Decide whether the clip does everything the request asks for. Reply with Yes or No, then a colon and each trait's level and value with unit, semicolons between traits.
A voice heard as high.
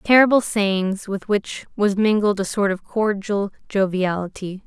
Yes: high, 200 Hz